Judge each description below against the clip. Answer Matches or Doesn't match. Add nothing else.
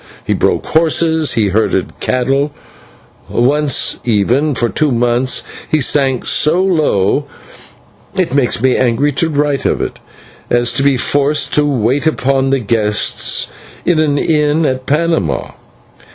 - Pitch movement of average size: Matches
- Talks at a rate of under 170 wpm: Matches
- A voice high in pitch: Doesn't match